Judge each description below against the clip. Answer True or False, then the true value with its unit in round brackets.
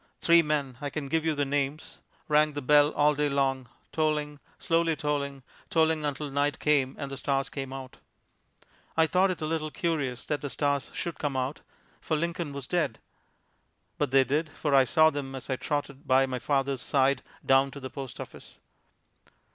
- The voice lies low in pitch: False (145 Hz)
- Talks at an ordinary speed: True (185 wpm)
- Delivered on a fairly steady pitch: True (2.2 semitones)